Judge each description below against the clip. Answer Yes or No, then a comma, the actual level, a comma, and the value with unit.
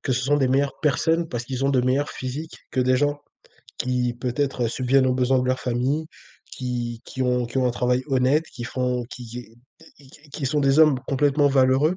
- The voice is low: Yes, low, 130 Hz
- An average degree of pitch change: No, narrow, 2.2 semitones